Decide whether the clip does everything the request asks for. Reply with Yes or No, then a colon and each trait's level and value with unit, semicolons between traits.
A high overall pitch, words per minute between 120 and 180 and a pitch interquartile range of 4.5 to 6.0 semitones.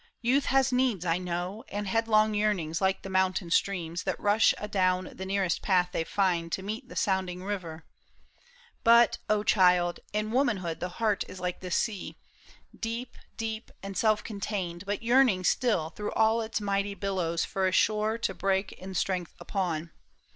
No: high, 195 Hz; average, 170 wpm; average, 3.1 semitones